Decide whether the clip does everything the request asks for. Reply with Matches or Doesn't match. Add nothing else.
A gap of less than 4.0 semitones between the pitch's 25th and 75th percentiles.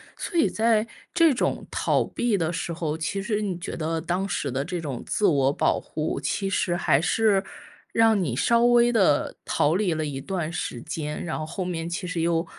Doesn't match